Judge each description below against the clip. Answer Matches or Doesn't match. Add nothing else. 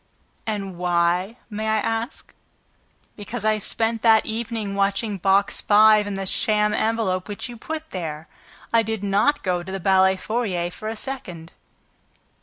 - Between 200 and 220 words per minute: Doesn't match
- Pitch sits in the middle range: Doesn't match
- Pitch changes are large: Doesn't match